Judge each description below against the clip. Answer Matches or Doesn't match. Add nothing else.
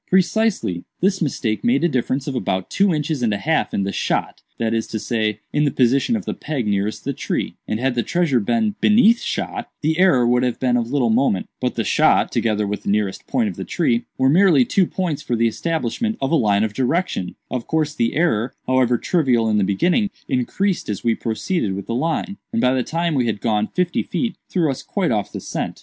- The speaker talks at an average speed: Doesn't match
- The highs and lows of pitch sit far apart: Matches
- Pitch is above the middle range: Doesn't match